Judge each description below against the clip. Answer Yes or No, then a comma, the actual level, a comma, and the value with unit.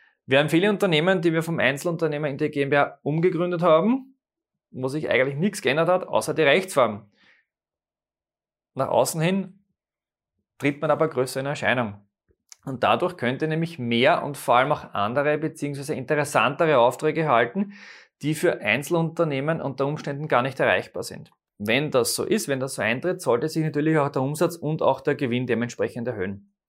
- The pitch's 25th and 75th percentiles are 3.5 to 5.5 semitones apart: Yes, average, 4.3 semitones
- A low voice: No, medium, 150 Hz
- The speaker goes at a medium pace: Yes, average, 165 wpm